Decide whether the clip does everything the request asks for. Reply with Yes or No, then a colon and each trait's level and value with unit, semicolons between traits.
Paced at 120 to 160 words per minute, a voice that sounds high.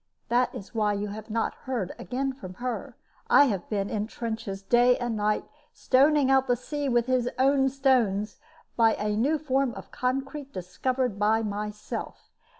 No: average, 170 wpm; high, 240 Hz